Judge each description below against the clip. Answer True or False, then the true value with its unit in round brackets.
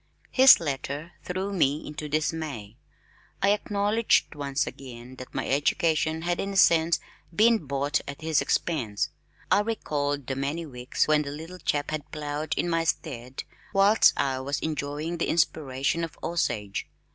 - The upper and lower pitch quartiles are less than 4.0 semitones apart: True (3.4 semitones)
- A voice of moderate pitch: True (155 Hz)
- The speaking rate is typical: True (155 wpm)